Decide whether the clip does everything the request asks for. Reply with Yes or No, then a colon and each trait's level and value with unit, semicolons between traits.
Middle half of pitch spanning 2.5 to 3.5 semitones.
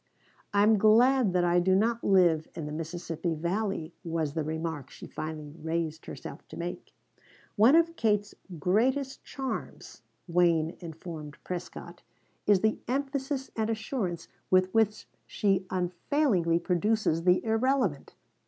No: average, 5.1 semitones